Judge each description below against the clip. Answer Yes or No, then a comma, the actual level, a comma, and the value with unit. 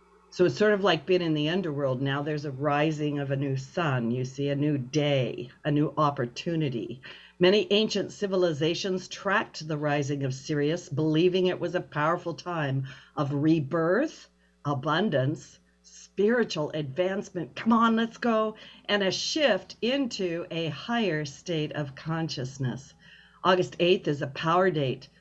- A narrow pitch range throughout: No, average, 4.4 semitones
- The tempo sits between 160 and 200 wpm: No, average, 150 wpm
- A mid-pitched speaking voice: Yes, medium, 160 Hz